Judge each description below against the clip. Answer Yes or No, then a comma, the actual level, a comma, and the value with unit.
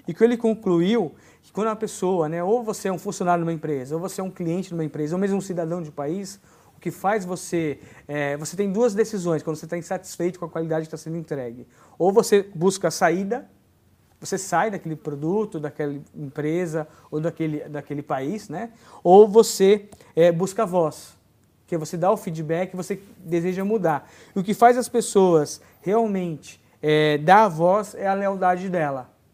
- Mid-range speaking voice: Yes, medium, 175 Hz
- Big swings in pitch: No, average, 4.0 semitones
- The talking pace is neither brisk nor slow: No, fast, 200 wpm